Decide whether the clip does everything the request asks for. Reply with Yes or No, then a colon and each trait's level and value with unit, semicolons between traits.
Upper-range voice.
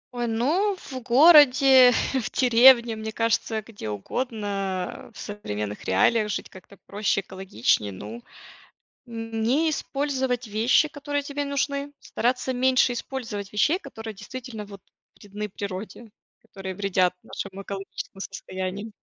Yes: high, 225 Hz